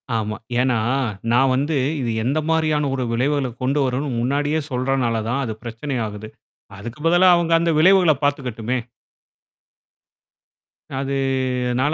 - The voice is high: No, low, 130 Hz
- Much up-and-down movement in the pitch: No, average, 3.5 semitones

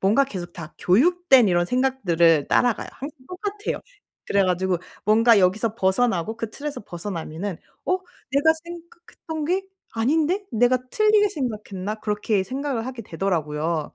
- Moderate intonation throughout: No, wide, 7.7 semitones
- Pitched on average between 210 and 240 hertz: Yes, high, 225 Hz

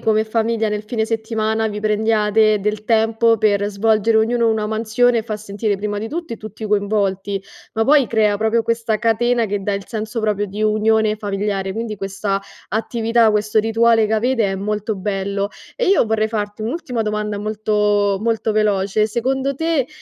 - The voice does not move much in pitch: Yes, narrow, 1.4 semitones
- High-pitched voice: Yes, high, 215 Hz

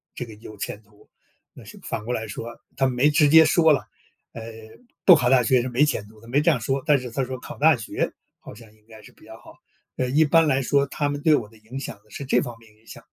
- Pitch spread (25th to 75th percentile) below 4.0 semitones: No, average, 4.4 semitones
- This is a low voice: Yes, low, 125 Hz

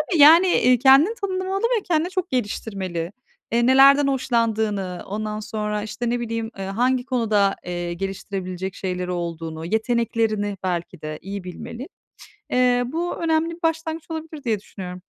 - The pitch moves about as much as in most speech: No, wide, 6.8 semitones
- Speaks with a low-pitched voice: No, high, 230 Hz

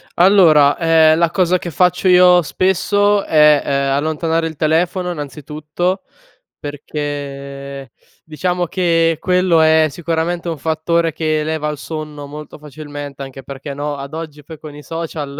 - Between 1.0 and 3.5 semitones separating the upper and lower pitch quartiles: Yes, average, 2.7 semitones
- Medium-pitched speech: Yes, medium, 155 Hz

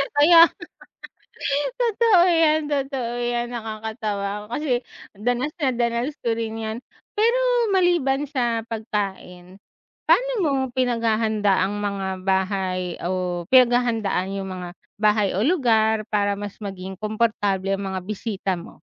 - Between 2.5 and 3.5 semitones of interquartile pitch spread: No, average, 4.3 semitones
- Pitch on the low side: No, high, 220 Hz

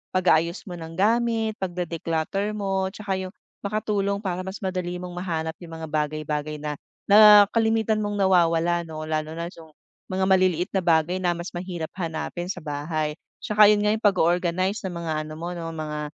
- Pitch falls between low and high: Yes, medium, 175 Hz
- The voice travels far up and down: No, average, 3.5 semitones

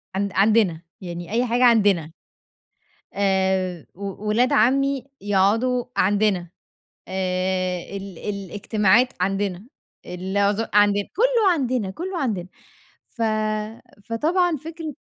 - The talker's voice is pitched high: Yes, high, 205 Hz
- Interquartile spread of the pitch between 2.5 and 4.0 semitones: No, average, 4.6 semitones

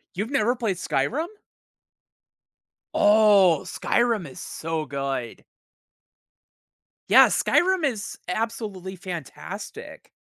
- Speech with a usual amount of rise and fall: No, wide, 6.0 semitones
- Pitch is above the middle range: Yes, high, 200 Hz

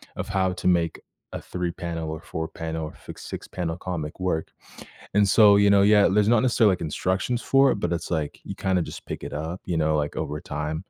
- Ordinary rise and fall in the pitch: Yes, average, 3.8 semitones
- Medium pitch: No, very low, 90 Hz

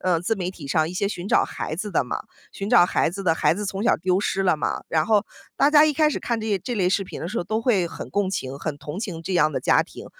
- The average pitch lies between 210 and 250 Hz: No, high, 190 Hz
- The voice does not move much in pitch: No, average, 3.9 semitones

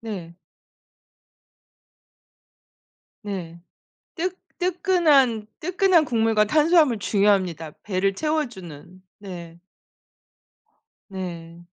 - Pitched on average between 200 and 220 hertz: Yes, high, 210 Hz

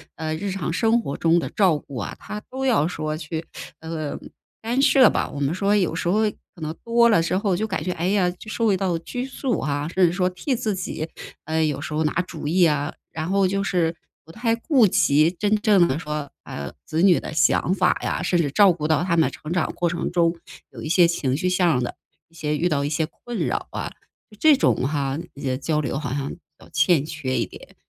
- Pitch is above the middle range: No, medium, 170 Hz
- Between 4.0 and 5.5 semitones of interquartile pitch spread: Yes, average, 4.4 semitones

